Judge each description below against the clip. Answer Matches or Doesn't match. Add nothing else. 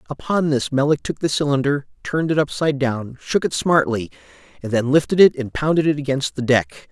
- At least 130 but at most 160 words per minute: Doesn't match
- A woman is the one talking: Doesn't match